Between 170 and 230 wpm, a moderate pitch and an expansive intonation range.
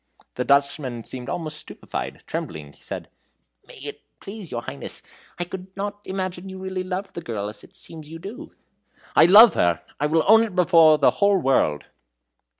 Yes: average, 180 wpm; medium, 175 Hz; wide, 5.8 semitones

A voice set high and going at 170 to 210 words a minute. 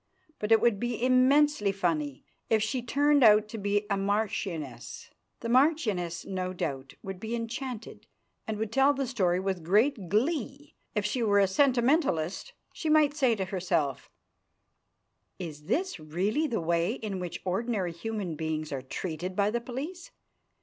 No: high, 210 Hz; average, 155 wpm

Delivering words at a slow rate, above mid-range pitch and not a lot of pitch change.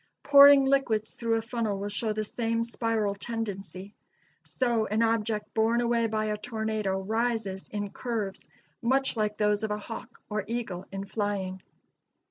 No: average, 155 wpm; high, 220 Hz; narrow, 2.1 semitones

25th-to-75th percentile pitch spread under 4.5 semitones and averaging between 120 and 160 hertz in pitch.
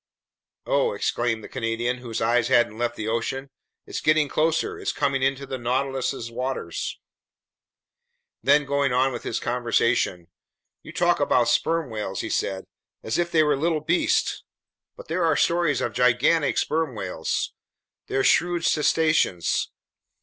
No: average, 4.8 semitones; low, 135 Hz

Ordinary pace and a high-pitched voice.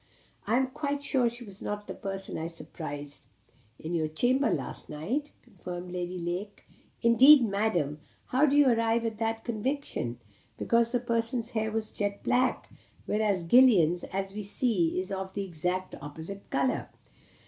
Yes: average, 160 wpm; high, 210 Hz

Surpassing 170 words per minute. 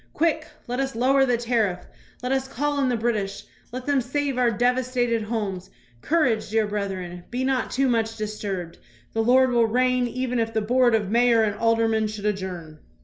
Yes: average, 185 wpm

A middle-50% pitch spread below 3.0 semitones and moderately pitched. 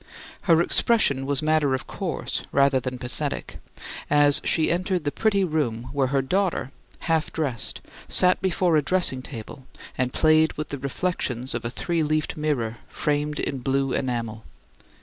No: average, 3.6 semitones; medium, 145 Hz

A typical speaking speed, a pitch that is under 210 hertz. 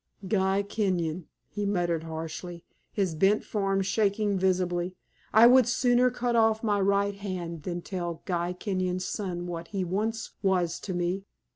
Yes: average, 150 wpm; high, 190 Hz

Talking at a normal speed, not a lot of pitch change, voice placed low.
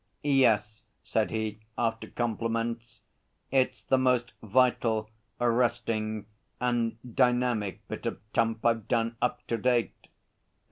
No: slow, 110 wpm; narrow, 1.7 semitones; low, 115 Hz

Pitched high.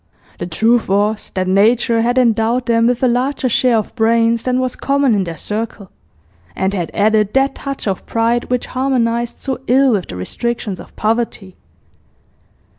Yes: high, 230 Hz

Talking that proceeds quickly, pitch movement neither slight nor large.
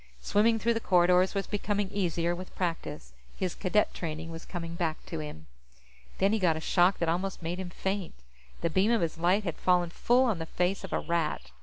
Yes: fast, 210 wpm; average, 3.0 semitones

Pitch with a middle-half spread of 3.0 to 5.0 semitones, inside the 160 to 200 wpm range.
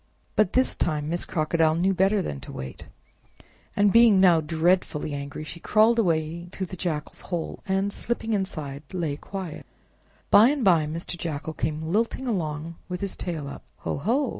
Yes: average, 4.2 semitones; average, 170 wpm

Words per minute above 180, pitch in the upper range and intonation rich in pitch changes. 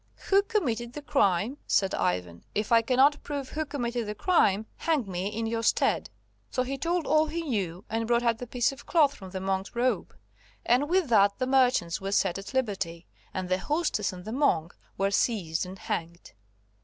Yes: average, 195 wpm; high, 230 Hz; wide, 6.3 semitones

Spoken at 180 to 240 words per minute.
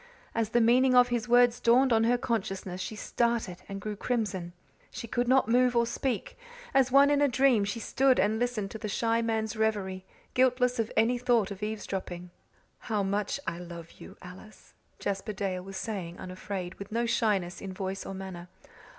Yes: average, 185 wpm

